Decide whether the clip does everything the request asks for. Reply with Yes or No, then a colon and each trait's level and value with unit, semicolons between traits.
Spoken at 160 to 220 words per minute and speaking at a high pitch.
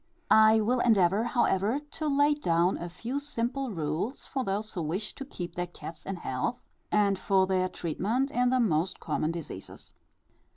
Yes: average, 170 wpm; high, 205 Hz